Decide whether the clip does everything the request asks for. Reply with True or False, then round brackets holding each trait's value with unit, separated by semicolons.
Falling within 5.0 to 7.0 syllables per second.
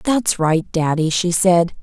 False (3.6 syllables/s)